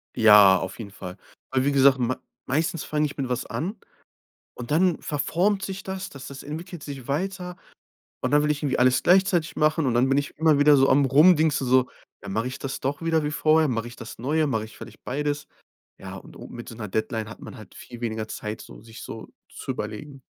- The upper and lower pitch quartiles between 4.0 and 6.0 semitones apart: Yes, average, 4.7 semitones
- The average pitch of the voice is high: No, medium, 140 Hz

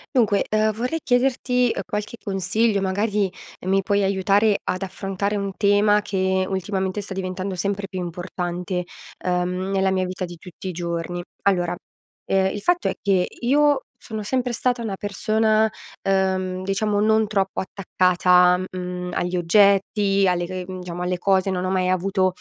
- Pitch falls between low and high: No, high, 195 Hz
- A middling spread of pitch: No, narrow, 2.2 semitones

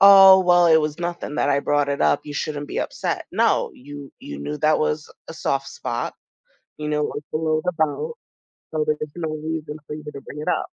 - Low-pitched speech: No, medium, 150 Hz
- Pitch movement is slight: Yes, narrow, 1.8 semitones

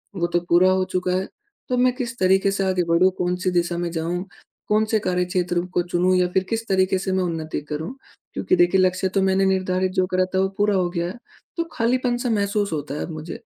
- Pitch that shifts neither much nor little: No, narrow, 2.1 semitones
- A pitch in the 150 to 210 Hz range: Yes, medium, 185 Hz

